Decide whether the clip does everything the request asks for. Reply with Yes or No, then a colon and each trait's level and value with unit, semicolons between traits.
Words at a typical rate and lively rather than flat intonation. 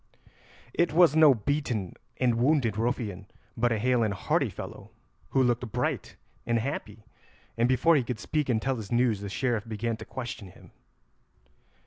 No: average, 165 wpm; average, 3.2 semitones